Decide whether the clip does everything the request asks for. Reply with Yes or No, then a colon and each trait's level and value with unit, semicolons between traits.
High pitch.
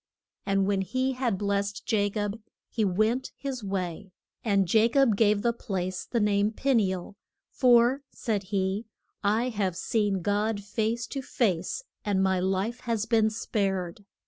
Yes: high, 205 Hz